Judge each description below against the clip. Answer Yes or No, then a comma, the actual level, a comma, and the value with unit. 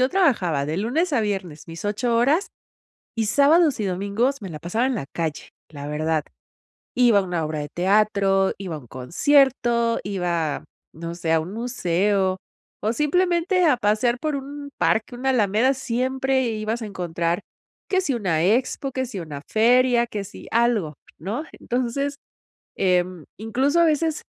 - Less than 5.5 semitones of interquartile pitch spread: No, wide, 6.7 semitones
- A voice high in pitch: Yes, high, 220 Hz